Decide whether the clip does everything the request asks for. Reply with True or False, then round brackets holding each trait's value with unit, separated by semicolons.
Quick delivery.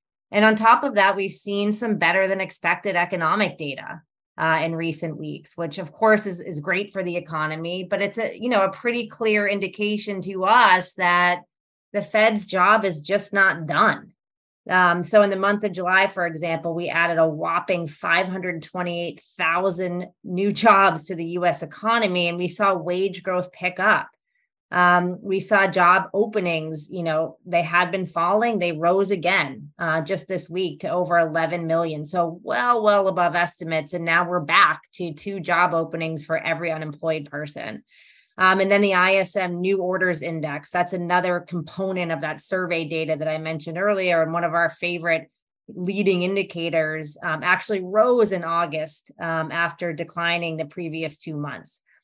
False (170 wpm)